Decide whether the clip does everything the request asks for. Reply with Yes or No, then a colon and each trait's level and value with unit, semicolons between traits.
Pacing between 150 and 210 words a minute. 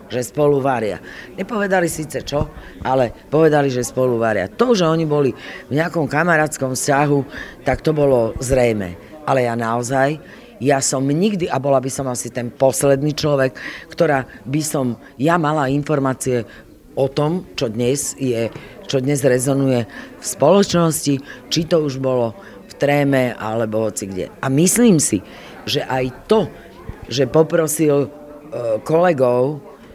No: average, 140 wpm